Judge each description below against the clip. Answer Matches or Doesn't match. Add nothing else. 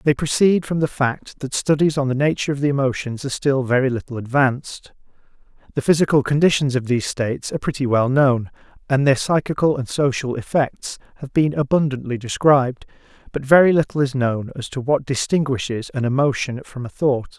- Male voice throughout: Matches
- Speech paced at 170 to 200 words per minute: Matches